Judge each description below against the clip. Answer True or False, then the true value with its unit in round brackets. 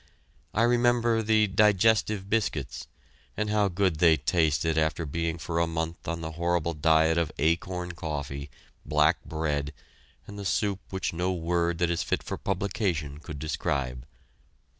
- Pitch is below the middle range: True (85 Hz)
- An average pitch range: True (3.9 semitones)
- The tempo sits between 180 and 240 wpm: False (150 wpm)